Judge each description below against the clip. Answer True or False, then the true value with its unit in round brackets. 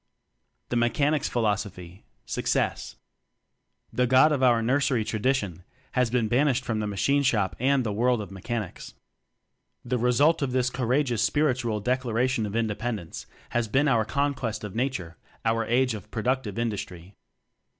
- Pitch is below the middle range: True (120 Hz)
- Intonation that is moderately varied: True (3.3 semitones)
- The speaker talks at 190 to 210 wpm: False (165 wpm)